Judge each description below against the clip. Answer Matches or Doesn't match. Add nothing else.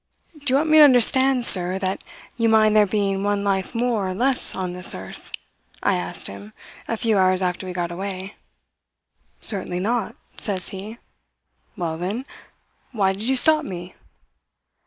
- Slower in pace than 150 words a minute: Doesn't match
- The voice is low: Doesn't match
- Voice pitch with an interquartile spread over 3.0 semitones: Matches